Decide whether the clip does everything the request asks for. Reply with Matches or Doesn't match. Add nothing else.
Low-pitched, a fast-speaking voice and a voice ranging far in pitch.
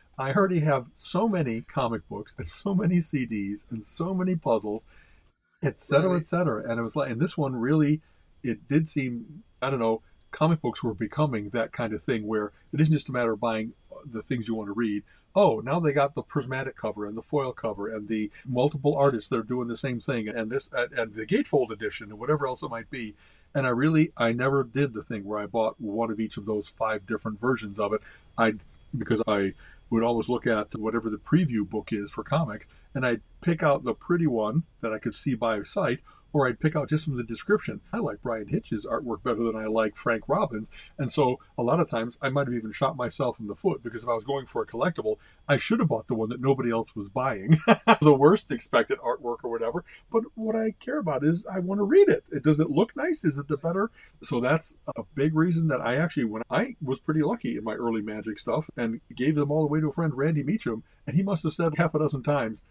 Matches